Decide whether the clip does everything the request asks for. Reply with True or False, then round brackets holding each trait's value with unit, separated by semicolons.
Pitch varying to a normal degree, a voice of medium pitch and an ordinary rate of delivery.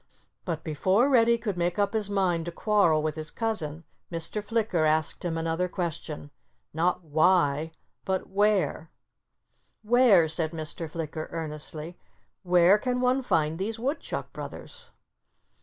False (4.8 semitones; 175 Hz; 125 wpm)